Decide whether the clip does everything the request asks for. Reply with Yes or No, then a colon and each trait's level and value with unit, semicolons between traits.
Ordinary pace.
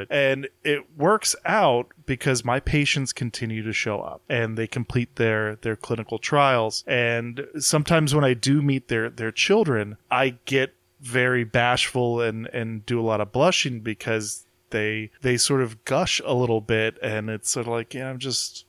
Yes: average, 185 wpm